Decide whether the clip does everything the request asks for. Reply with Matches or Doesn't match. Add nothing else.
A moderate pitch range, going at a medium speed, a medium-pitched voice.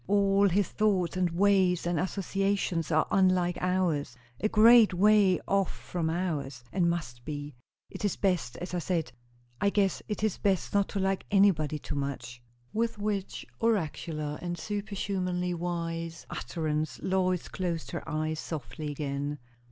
Matches